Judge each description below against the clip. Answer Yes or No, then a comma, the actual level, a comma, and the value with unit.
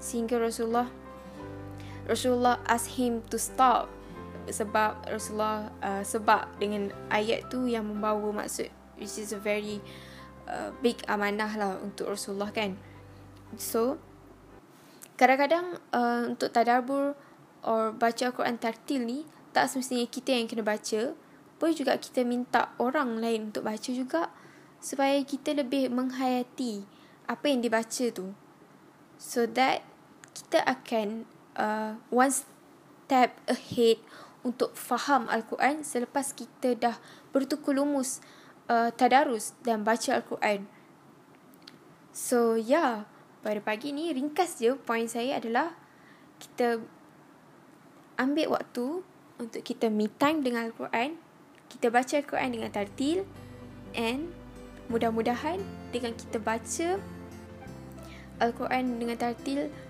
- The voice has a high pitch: Yes, high, 235 Hz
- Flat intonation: No, average, 3.2 semitones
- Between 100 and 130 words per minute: Yes, average, 115 wpm